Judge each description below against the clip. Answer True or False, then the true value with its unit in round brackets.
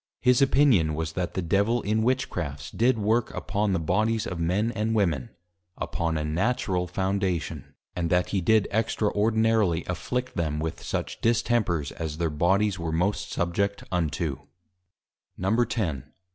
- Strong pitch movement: False (4.9 semitones)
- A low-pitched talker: True (95 Hz)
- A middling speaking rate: True (145 wpm)